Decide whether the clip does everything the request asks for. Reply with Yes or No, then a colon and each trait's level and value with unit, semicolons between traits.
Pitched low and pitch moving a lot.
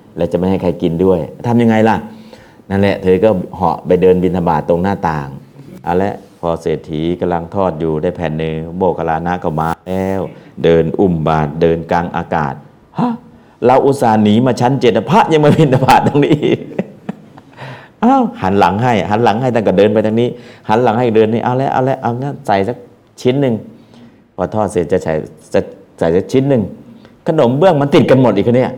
Yes: low, 100 Hz; wide, 6.0 semitones